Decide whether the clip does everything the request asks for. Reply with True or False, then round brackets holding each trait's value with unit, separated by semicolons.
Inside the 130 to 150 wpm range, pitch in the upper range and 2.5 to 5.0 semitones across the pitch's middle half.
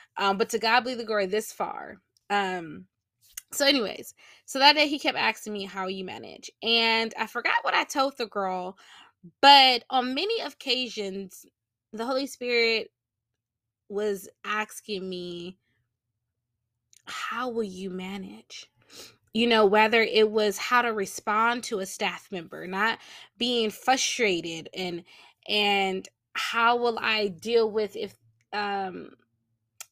True (140 wpm; 210 Hz; 4.4 semitones)